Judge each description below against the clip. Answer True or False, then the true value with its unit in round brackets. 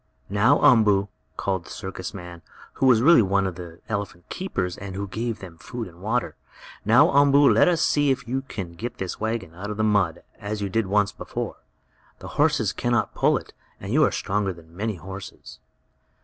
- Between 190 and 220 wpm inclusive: True (200 wpm)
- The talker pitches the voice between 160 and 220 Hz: False (100 Hz)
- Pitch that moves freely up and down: False (4.0 semitones)